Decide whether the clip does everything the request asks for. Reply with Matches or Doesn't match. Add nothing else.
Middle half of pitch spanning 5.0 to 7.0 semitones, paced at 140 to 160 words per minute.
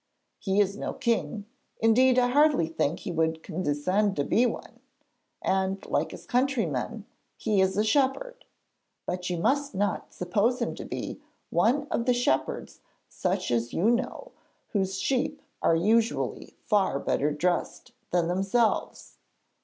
Matches